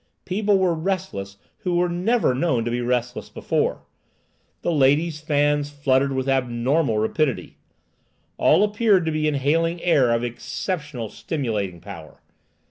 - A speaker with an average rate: No, slow, 130 wpm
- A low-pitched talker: No, medium, 145 Hz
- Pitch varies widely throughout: Yes, wide, 5.7 semitones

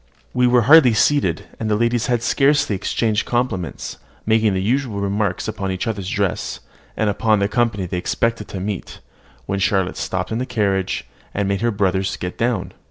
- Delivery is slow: No, average, 175 wpm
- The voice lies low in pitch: Yes, low, 105 Hz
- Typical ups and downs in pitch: Yes, average, 3.3 semitones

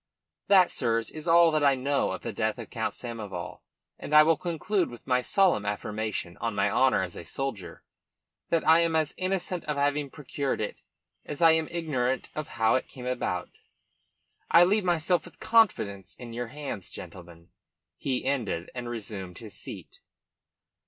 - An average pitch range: No, wide, 6.8 semitones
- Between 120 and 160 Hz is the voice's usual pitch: Yes, low, 135 Hz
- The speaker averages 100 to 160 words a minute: No, average, 170 wpm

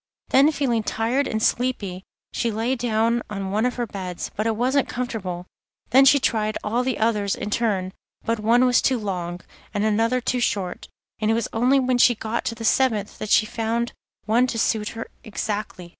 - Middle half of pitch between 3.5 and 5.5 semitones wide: No, average, 2.8 semitones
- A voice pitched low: No, high, 225 Hz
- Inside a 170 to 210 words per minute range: Yes, average, 195 wpm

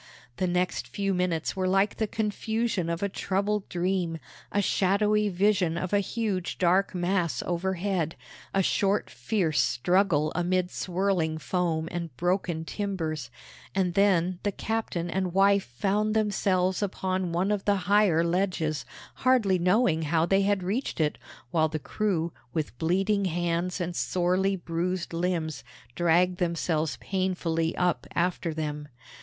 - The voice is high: No, medium, 180 Hz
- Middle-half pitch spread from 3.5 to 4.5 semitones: No, average, 2.8 semitones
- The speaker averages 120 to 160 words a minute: Yes, average, 140 wpm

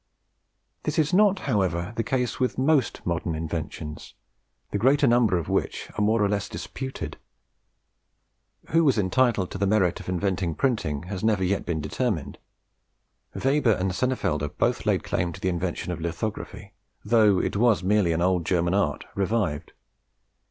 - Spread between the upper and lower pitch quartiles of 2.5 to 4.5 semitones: No, wide, 5.6 semitones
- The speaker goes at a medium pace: Yes, average, 160 wpm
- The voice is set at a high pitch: No, low, 100 Hz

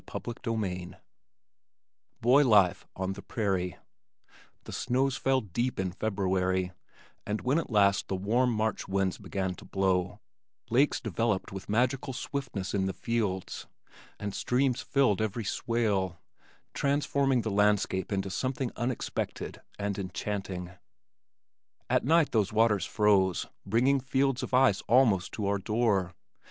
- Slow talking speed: Yes, slow, 130 wpm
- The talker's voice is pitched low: Yes, low, 105 Hz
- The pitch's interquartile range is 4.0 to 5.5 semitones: Yes, average, 4.5 semitones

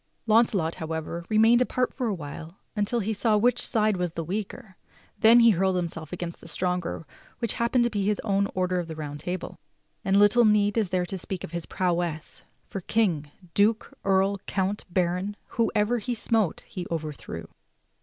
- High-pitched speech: Yes, high, 195 Hz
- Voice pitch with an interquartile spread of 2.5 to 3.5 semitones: No, average, 3.9 semitones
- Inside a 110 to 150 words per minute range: No, average, 185 wpm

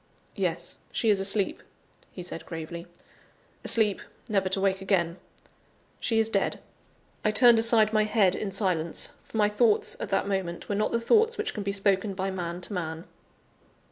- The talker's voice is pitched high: Yes, high, 195 Hz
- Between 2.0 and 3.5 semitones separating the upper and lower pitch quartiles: Yes, average, 2.7 semitones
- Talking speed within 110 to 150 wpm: No, average, 175 wpm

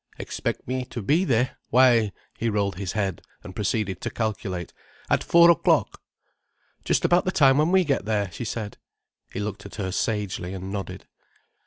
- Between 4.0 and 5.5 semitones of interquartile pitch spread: Yes, average, 4.8 semitones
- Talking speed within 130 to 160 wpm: No, average, 175 wpm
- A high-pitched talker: No, low, 105 Hz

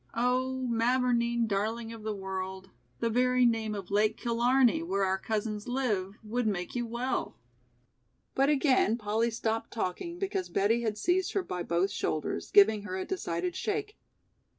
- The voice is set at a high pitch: Yes, high, 225 Hz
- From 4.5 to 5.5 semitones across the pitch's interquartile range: No, average, 4.0 semitones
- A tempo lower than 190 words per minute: Yes, average, 155 wpm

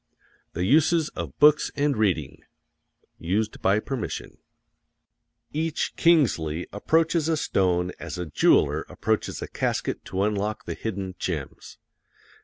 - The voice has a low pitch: Yes, low, 105 Hz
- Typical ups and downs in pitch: No, wide, 8.8 semitones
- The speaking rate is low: Yes, slow, 105 wpm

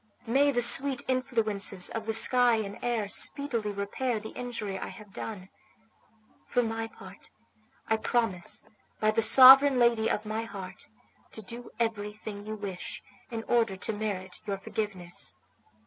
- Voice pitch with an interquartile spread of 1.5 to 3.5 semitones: Yes, average, 2.9 semitones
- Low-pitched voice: No, high, 220 Hz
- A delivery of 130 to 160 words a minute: Yes, average, 150 wpm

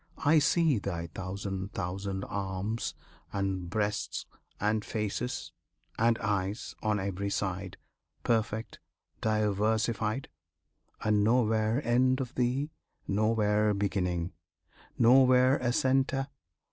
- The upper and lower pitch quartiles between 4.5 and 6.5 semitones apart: No, average, 3.5 semitones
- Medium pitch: No, low, 105 Hz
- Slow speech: Yes, slow, 95 wpm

